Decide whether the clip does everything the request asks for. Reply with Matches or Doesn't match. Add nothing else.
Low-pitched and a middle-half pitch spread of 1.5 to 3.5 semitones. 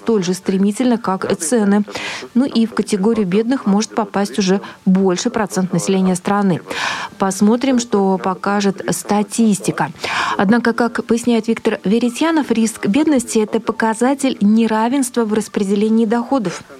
Doesn't match